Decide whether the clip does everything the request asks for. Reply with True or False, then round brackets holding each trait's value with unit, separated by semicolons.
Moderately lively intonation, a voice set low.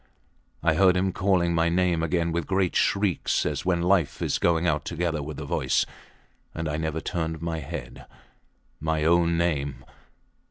False (1.8 semitones; 85 Hz)